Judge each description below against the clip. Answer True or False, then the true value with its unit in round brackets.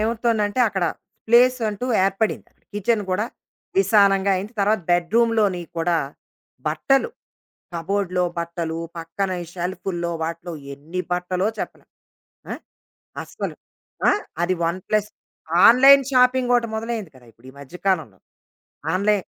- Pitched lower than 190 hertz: False (195 Hz)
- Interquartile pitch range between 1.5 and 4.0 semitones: False (4.6 semitones)